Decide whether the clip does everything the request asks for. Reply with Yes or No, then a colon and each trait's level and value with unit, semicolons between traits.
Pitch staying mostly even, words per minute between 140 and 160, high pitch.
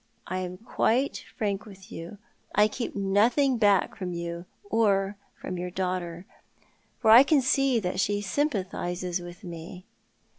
No: average, 3.7 semitones; average, 145 wpm; high, 195 Hz